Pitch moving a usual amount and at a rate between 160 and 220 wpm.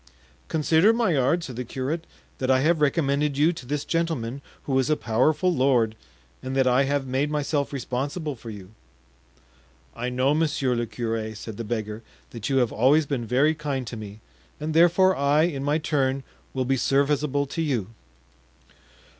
Yes: average, 3.4 semitones; average, 170 wpm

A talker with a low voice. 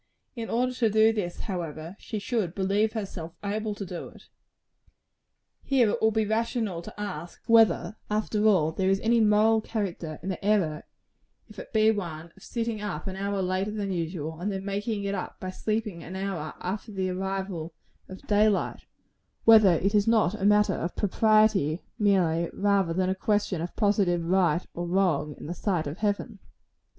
No: high, 200 Hz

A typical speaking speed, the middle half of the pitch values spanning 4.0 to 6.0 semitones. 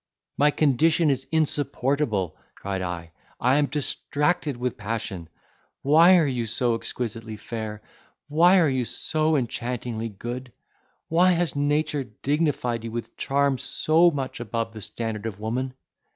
No: slow, 130 wpm; average, 4.7 semitones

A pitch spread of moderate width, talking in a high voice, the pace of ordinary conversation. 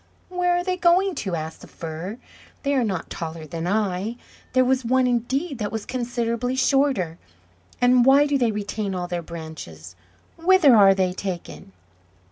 No: wide, 7.1 semitones; high, 225 Hz; average, 165 wpm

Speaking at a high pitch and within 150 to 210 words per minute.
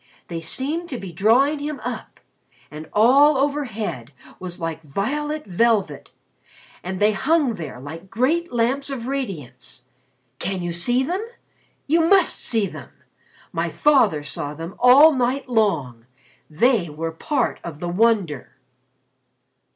No: high, 220 Hz; slow, 135 wpm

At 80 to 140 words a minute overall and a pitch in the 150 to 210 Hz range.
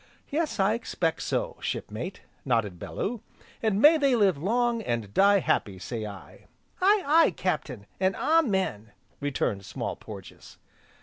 Yes: slow, 135 wpm; high, 190 Hz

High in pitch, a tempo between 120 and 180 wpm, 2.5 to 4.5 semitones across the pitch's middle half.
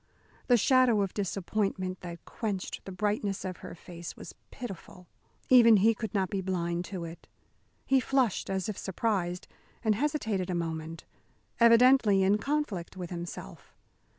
Yes: high, 195 Hz; average, 150 wpm; average, 4.1 semitones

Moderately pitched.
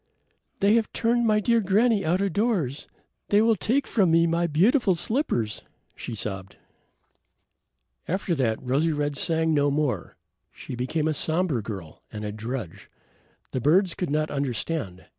Yes: medium, 160 Hz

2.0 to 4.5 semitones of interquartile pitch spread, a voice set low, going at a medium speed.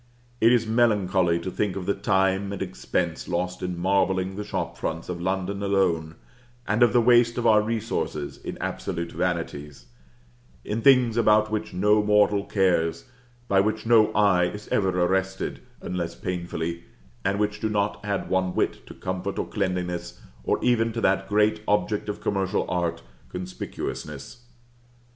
Yes: average, 2.9 semitones; very low, 95 Hz; average, 155 wpm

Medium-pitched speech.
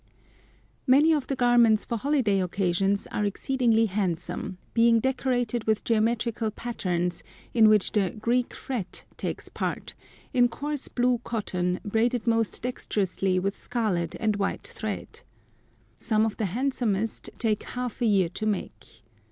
No: high, 220 Hz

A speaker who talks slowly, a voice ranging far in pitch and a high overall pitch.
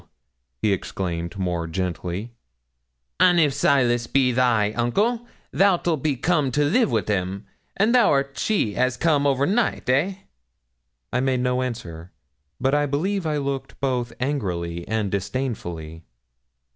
No: slow, 130 wpm; wide, 6.7 semitones; low, 125 Hz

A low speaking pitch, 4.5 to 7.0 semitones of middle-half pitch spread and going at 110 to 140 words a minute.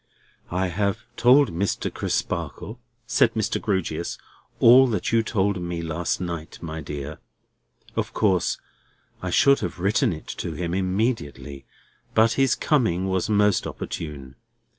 Yes: very low, 95 Hz; average, 4.9 semitones; slow, 135 wpm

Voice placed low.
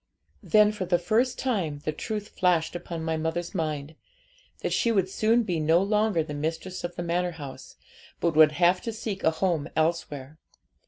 No: medium, 175 Hz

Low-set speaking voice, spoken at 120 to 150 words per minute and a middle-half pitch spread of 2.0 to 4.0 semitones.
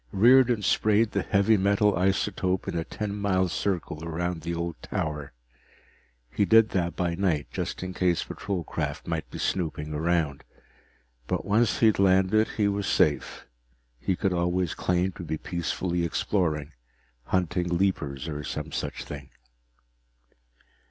Yes: very low, 90 Hz; average, 145 wpm; average, 3.2 semitones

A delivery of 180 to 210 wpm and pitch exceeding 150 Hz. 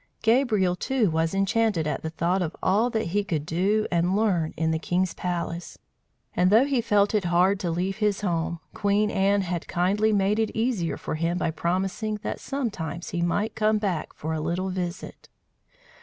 Yes: average, 185 wpm; high, 190 Hz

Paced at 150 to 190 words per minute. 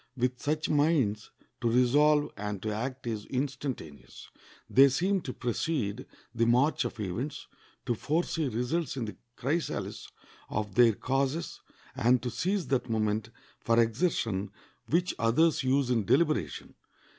No: slow, 135 wpm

